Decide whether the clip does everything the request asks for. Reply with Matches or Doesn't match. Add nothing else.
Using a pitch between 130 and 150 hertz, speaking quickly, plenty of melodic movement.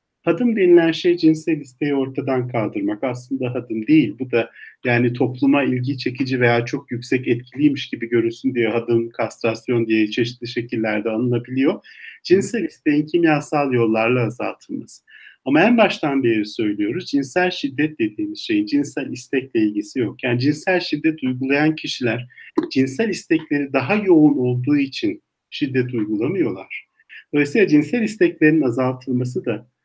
Doesn't match